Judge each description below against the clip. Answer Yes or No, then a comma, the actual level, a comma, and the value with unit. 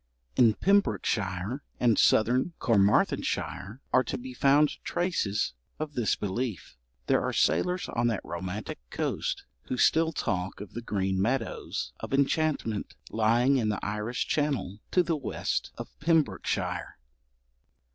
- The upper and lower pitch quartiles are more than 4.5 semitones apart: Yes, wide, 5.6 semitones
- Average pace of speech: No, slow, 130 wpm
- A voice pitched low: Yes, low, 120 Hz